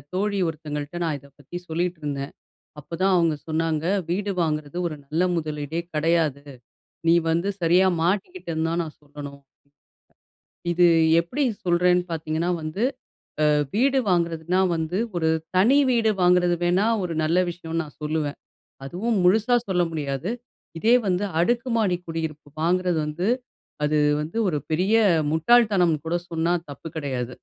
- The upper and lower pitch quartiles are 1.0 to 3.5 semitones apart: Yes, average, 2.8 semitones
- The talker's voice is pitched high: No, medium, 170 Hz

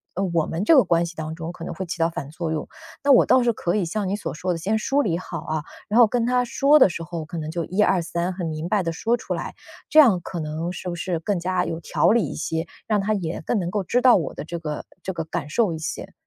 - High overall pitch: No, medium, 175 Hz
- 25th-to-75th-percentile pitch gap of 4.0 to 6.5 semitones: Yes, average, 4.4 semitones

